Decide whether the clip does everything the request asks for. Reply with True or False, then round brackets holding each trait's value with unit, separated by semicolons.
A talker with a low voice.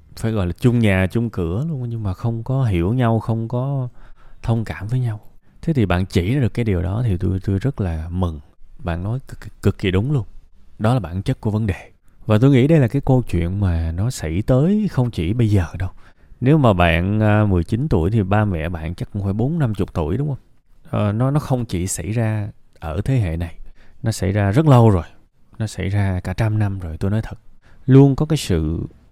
True (105 Hz)